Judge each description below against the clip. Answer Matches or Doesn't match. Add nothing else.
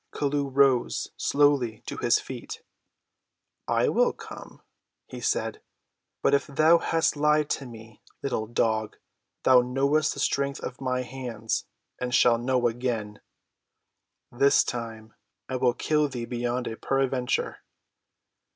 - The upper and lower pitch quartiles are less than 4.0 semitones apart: Matches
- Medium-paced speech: Doesn't match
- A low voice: Matches